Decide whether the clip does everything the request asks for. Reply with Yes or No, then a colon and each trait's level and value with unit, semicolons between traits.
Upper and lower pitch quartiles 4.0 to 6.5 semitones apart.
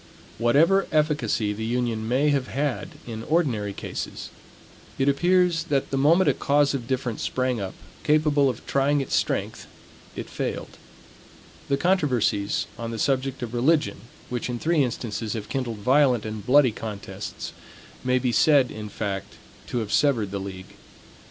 Yes: average, 4.6 semitones